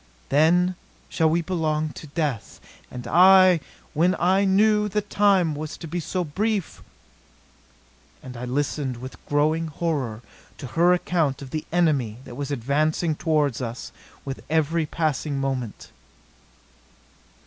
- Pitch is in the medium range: Yes, medium, 155 Hz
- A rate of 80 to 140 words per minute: Yes, slow, 135 wpm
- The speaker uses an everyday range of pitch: Yes, average, 4.1 semitones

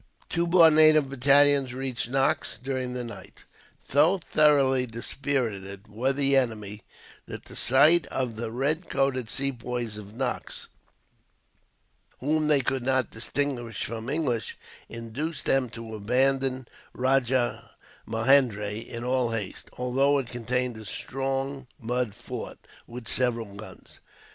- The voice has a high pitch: No, low, 130 Hz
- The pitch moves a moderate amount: Yes, average, 3.0 semitones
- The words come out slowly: Yes, slow, 125 wpm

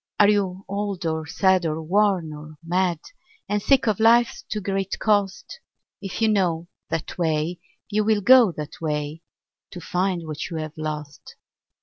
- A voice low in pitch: No, medium, 180 Hz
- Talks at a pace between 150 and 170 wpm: Yes, average, 160 wpm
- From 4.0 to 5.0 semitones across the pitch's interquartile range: Yes, average, 4.4 semitones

